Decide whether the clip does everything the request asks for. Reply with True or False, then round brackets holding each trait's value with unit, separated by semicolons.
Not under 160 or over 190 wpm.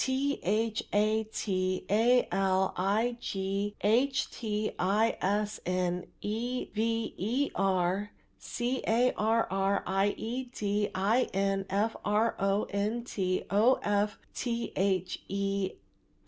False (135 wpm)